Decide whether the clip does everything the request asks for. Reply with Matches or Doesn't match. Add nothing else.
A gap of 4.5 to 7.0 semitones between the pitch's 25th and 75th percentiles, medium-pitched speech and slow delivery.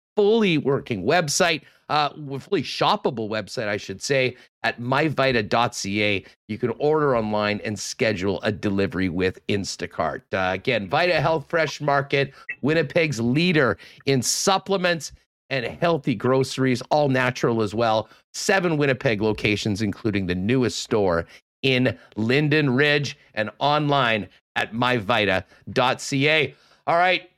Doesn't match